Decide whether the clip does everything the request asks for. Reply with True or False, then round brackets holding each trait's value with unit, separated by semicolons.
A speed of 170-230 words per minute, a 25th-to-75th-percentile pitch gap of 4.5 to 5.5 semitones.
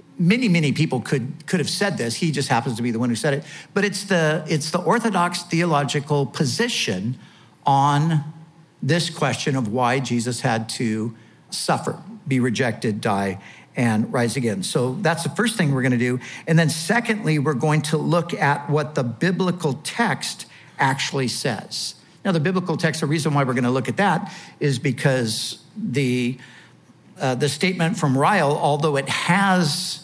True (175 wpm; 4.8 semitones)